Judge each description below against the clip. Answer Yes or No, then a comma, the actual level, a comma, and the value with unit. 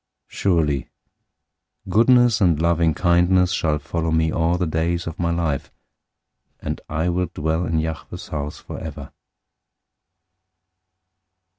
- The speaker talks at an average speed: No, slow, 120 wpm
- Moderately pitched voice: No, very low, 85 Hz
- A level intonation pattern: Yes, narrow, 1.9 semitones